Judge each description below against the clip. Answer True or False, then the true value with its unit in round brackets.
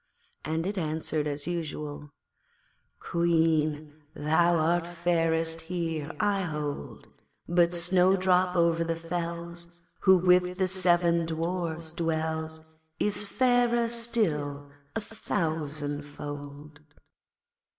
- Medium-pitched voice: True (165 Hz)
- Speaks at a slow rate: True (95 wpm)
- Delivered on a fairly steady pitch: True (2.3 semitones)